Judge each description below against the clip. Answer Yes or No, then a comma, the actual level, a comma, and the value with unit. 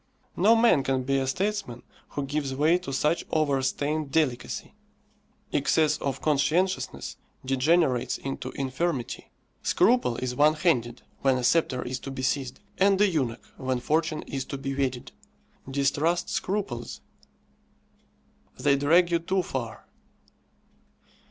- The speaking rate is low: Yes, slow, 130 wpm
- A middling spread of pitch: Yes, average, 4.1 semitones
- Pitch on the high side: No, medium, 140 Hz